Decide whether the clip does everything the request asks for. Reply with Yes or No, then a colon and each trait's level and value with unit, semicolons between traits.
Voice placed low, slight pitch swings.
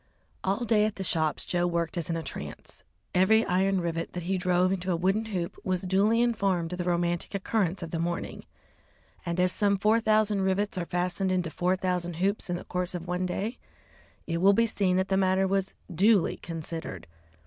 No: medium, 185 Hz; narrow, 2.2 semitones